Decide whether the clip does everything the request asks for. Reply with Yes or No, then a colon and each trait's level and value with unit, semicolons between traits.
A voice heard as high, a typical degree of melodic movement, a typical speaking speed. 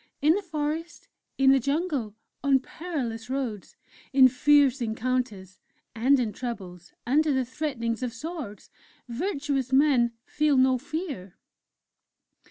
No: very high, 265 Hz; average, 4.0 semitones; slow, 120 wpm